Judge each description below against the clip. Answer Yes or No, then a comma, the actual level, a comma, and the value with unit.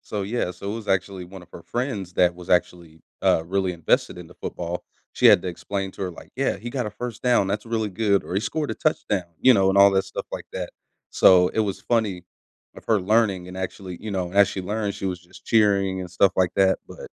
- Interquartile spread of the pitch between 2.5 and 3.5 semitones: Yes, average, 2.9 semitones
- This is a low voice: Yes, very low, 95 Hz